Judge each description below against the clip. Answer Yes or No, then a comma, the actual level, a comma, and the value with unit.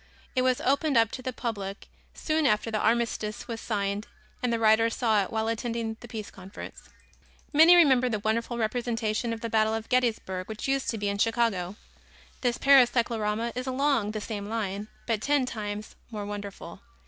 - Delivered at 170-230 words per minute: Yes, average, 185 wpm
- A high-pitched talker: Yes, high, 225 Hz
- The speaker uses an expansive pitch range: No, narrow, 2.6 semitones